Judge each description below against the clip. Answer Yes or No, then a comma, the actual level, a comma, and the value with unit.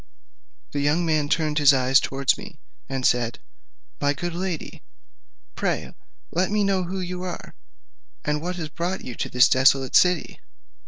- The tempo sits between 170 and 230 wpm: No, average, 160 wpm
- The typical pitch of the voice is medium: Yes, medium, 155 Hz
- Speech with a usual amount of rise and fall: Yes, average, 4.7 semitones